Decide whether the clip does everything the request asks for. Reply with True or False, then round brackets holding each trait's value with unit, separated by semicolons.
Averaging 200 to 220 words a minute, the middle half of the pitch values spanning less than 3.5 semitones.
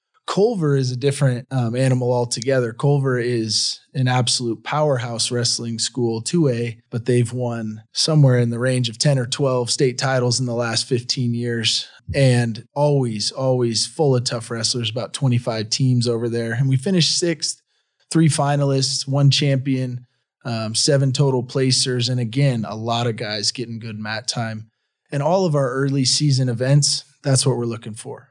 False (165 wpm; 2.7 semitones)